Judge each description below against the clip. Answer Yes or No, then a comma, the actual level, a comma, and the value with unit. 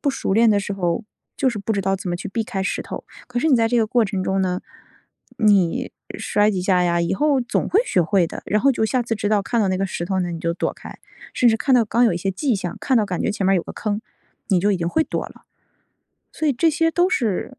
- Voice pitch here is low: No, high, 205 Hz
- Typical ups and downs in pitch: Yes, average, 4.3 semitones